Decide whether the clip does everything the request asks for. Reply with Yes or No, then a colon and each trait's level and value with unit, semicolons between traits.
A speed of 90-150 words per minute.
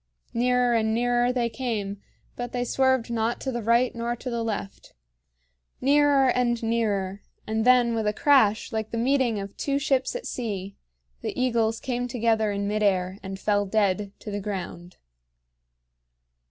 No: average, 165 wpm